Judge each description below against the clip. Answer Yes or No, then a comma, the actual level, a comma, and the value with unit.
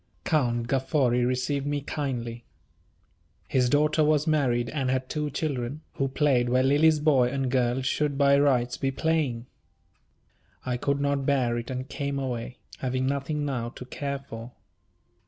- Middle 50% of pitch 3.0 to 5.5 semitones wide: No, narrow, 2.6 semitones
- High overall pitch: No, low, 135 Hz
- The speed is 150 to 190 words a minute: Yes, average, 155 wpm